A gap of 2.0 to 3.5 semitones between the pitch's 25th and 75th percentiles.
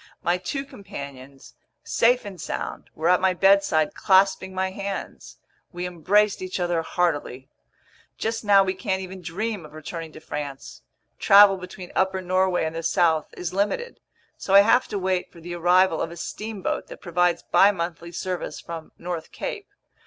Yes: average, 2.7 semitones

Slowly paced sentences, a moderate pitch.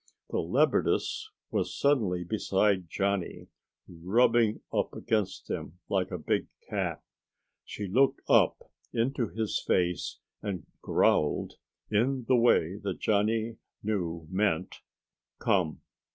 No: slow, 110 wpm; low, 100 Hz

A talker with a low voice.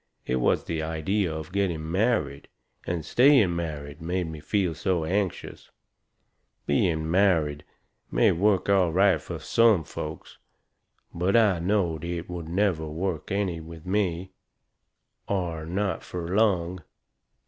Yes: very low, 85 Hz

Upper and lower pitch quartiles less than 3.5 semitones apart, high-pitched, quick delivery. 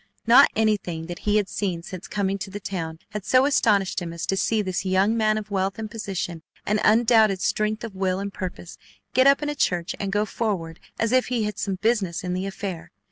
Yes: average, 2.8 semitones; high, 200 Hz; fast, 225 wpm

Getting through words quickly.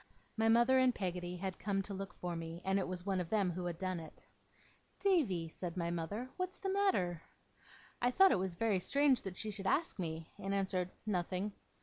Yes: fast, 210 wpm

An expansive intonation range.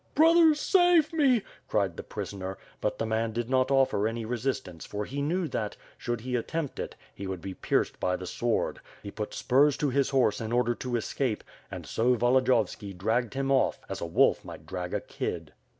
No: average, 4.7 semitones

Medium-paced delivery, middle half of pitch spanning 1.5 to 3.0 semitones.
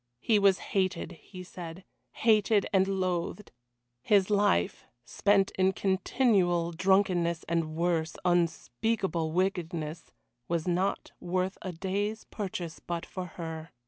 No: slow, 115 wpm; narrow, 2.6 semitones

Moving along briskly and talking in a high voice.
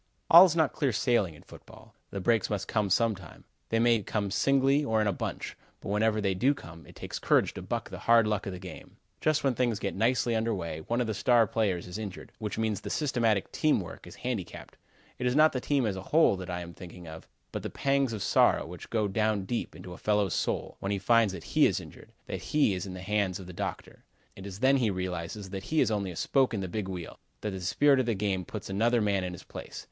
No: fast, 255 wpm; low, 105 Hz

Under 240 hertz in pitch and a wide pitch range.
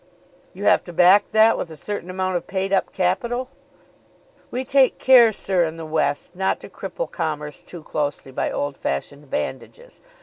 Yes: medium, 185 Hz; wide, 6.0 semitones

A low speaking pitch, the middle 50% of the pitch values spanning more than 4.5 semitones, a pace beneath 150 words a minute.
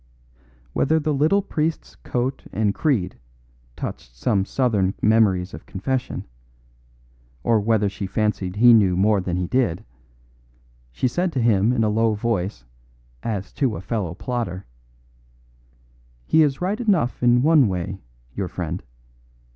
Yes: low, 110 Hz; wide, 5.4 semitones; average, 140 wpm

